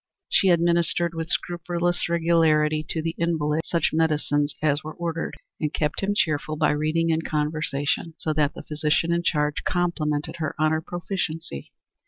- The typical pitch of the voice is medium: Yes, medium, 160 Hz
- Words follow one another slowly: No, average, 160 wpm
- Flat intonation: Yes, narrow, 1.9 semitones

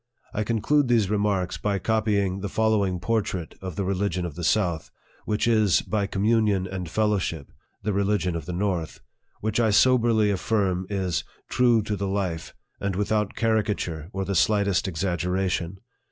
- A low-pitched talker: Yes, low, 100 Hz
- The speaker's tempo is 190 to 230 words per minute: No, average, 165 wpm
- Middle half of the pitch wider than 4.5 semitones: No, average, 2.8 semitones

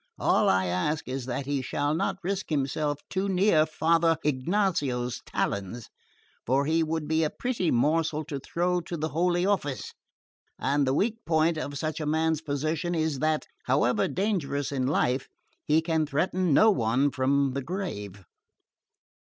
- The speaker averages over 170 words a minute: No, average, 160 wpm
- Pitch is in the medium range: Yes, medium, 155 Hz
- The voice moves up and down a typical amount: Yes, average, 3.5 semitones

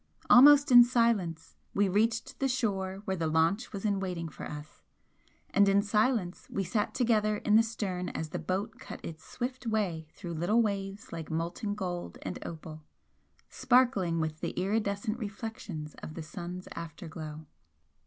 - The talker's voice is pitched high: Yes, high, 195 Hz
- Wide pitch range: No, average, 4.8 semitones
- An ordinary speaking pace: Yes, average, 165 wpm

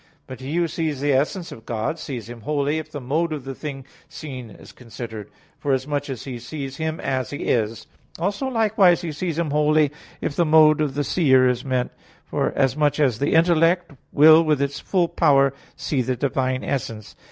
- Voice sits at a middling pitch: Yes, medium, 145 Hz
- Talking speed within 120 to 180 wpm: No, average, 190 wpm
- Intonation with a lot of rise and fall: No, average, 3.4 semitones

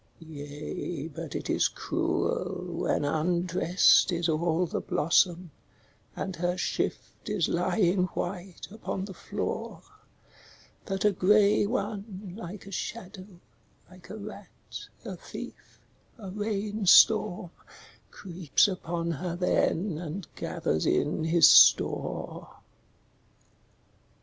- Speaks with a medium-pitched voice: Yes, medium, 180 Hz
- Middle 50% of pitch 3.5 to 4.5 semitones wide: No, average, 2.9 semitones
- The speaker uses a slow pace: Yes, slow, 110 wpm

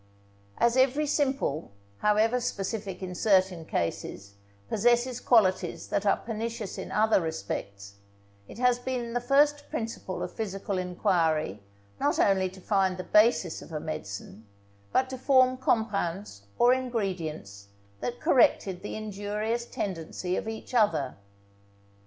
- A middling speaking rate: No, slow, 130 wpm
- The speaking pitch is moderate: No, high, 205 Hz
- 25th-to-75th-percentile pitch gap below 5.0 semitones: No, wide, 5.4 semitones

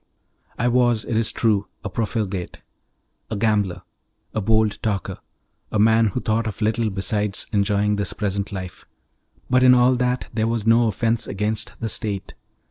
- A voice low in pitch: Yes, low, 110 Hz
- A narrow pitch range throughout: Yes, narrow, 2.1 semitones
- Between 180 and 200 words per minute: No, average, 160 wpm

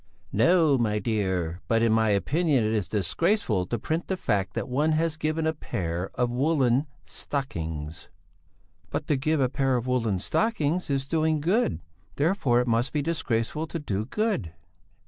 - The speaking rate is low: No, average, 165 wpm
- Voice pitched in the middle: No, low, 130 Hz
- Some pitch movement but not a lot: No, wide, 6.6 semitones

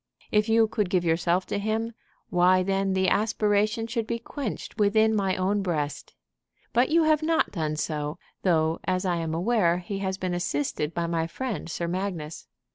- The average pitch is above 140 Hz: Yes, high, 190 Hz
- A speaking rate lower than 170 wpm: No, average, 180 wpm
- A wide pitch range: No, average, 4.3 semitones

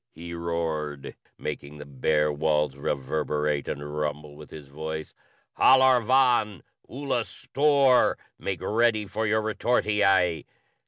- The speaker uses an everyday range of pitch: No, wide, 6.8 semitones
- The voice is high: No, very low, 85 Hz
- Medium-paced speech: No, slow, 125 wpm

